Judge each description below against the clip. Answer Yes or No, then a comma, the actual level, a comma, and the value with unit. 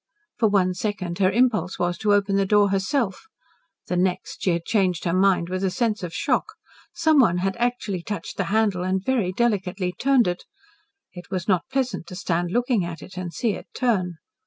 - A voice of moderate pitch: No, high, 195 Hz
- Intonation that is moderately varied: Yes, average, 3.6 semitones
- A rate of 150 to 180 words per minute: No, average, 195 wpm